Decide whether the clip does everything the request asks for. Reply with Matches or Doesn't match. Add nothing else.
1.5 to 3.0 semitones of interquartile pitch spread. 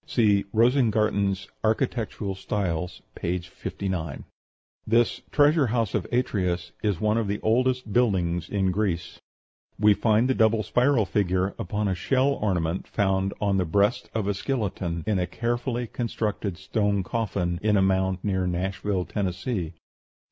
Doesn't match